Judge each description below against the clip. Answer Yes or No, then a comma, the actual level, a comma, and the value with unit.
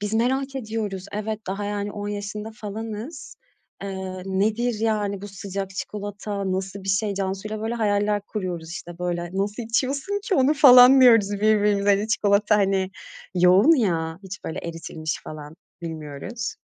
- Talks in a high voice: Yes, high, 205 Hz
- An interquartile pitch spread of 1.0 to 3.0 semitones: Yes, narrow, 2.6 semitones